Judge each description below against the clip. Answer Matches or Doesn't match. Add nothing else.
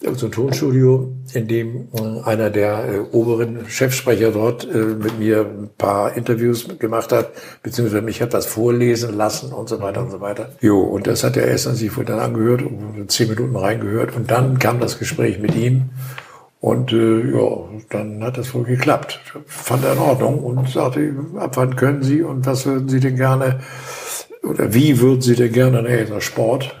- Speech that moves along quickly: Matches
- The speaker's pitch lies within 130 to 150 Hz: Doesn't match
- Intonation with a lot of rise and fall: Doesn't match